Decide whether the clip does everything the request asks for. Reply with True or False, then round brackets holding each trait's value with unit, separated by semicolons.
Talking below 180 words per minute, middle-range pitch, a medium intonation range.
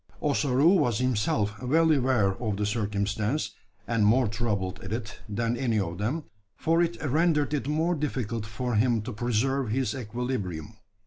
False (155 wpm; 120 Hz; 4.5 semitones)